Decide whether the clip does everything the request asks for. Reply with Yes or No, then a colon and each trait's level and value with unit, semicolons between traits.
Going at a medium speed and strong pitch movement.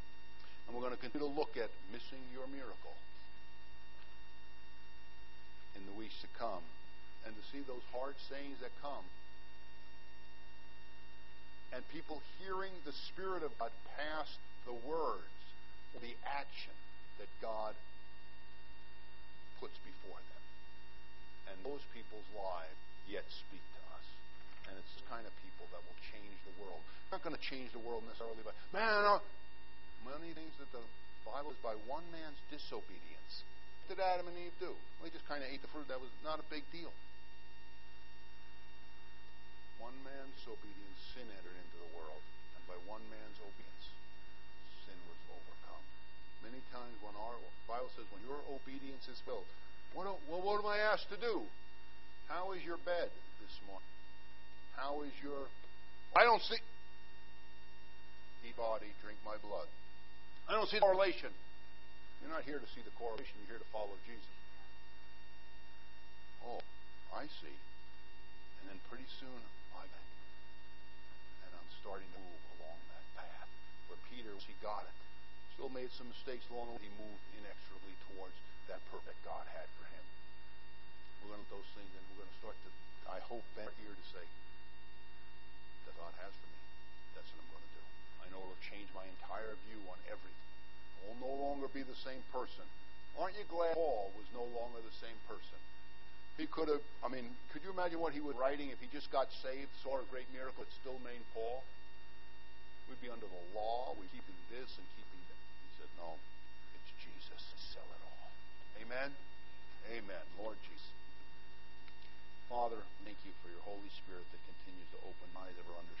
Yes: average, 170 wpm; wide, 6.7 semitones